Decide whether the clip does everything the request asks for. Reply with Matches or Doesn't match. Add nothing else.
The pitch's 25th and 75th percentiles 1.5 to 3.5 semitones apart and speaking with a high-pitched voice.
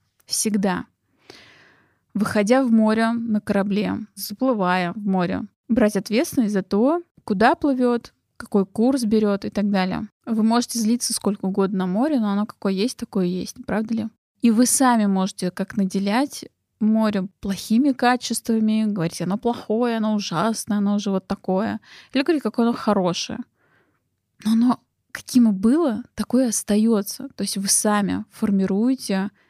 Matches